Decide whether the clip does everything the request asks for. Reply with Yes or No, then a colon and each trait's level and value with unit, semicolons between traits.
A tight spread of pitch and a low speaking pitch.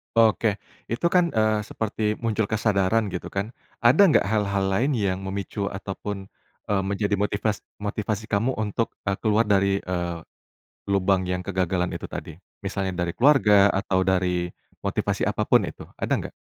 Yes: narrow, 2.3 semitones; low, 100 Hz